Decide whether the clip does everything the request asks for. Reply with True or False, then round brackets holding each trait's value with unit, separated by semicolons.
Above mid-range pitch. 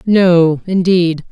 False (175 Hz)